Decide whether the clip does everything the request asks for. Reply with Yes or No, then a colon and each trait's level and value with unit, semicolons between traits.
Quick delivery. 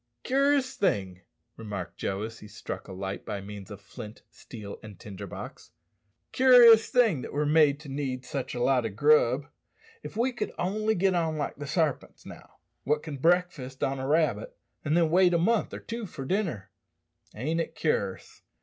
No: average, 185 wpm